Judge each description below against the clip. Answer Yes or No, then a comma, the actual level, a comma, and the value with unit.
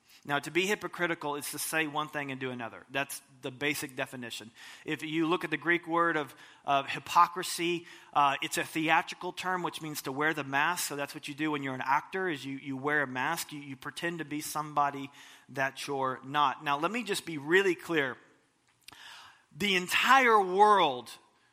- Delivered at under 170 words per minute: No, average, 200 wpm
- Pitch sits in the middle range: Yes, medium, 150 Hz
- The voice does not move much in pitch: No, average, 3.5 semitones